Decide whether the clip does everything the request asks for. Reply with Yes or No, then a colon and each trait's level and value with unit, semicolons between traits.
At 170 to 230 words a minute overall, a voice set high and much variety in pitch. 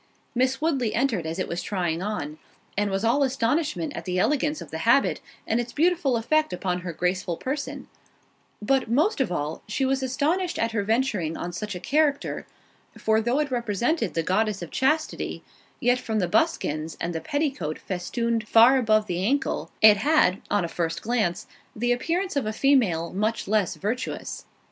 Yes: average, 175 wpm; high, 225 Hz; wide, 6.7 semitones